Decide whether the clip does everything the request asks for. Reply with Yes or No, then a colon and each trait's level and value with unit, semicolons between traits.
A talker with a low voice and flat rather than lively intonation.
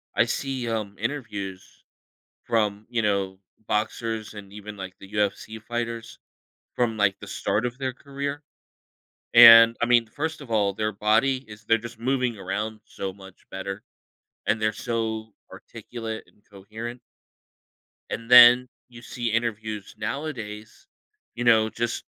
Yes: low, 110 Hz; narrow, 2.2 semitones